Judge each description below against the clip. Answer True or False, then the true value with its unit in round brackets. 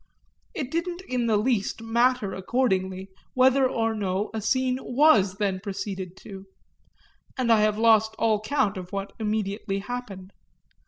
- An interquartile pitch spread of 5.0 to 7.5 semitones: False (4.1 semitones)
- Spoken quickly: False (145 wpm)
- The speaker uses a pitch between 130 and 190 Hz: False (220 Hz)